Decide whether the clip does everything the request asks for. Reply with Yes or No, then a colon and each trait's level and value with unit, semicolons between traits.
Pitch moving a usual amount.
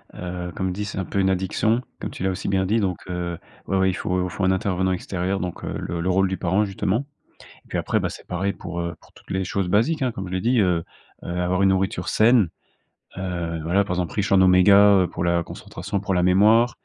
No: narrow, 1.8 semitones